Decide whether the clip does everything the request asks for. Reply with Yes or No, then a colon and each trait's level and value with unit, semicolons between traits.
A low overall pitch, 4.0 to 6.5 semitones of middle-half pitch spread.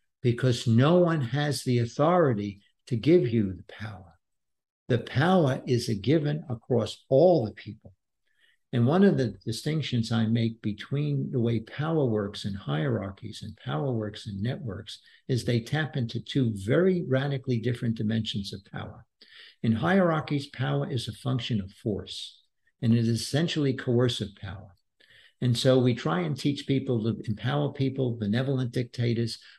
Yes: low, 120 Hz; average, 4.3 semitones